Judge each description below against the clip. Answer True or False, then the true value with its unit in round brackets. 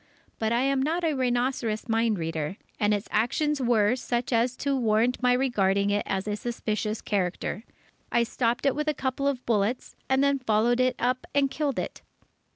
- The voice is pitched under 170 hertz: False (240 Hz)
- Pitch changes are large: False (3.8 semitones)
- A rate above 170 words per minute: True (185 wpm)